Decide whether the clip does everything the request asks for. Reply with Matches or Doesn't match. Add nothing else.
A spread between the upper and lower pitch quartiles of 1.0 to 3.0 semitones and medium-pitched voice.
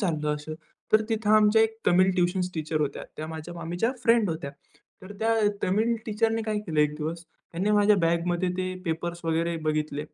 Doesn't match